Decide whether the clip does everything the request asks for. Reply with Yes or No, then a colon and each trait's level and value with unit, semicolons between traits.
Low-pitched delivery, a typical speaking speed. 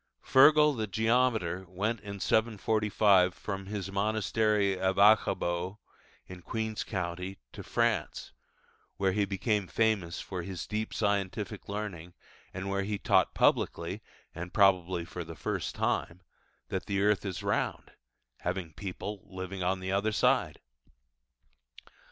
No: low, 100 Hz; slow, 130 wpm